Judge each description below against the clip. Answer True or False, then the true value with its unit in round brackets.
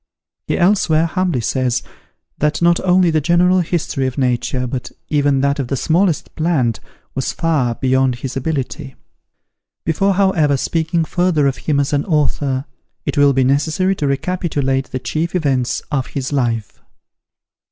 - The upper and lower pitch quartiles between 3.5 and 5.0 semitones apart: True (4.1 semitones)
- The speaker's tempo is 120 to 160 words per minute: True (150 wpm)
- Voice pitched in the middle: True (145 Hz)